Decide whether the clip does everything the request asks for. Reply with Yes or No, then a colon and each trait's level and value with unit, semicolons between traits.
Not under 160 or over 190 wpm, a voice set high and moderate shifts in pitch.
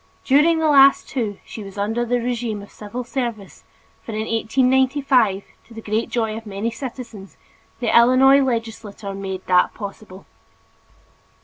No: average, 145 wpm; high, 230 Hz; average, 3.6 semitones